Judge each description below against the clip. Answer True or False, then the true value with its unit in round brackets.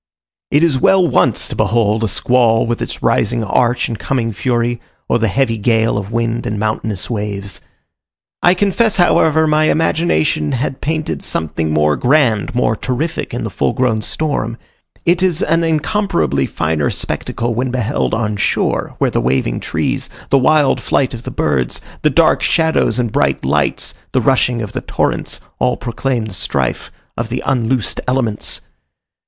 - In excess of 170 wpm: False (165 wpm)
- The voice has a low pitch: True (120 Hz)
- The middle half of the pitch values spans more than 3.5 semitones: True (5.2 semitones)